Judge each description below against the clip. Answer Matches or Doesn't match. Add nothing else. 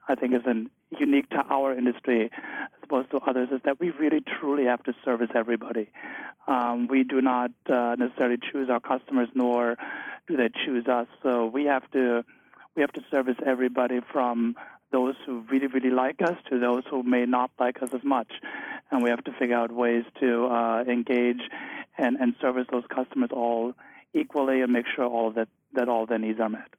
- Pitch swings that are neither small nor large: Doesn't match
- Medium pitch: Doesn't match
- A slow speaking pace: Doesn't match